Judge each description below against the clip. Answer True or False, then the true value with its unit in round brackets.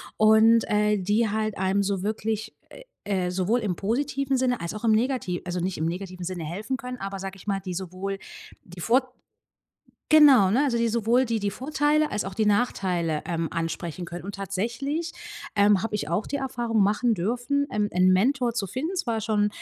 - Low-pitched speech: False (210 Hz)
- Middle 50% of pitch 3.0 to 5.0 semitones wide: True (4.5 semitones)